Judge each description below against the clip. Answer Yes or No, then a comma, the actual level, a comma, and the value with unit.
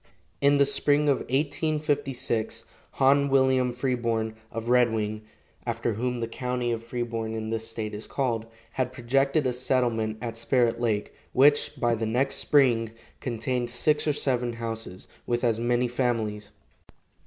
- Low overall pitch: Yes, low, 120 Hz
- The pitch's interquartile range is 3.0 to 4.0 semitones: No, narrow, 2.6 semitones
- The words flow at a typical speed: Yes, average, 150 wpm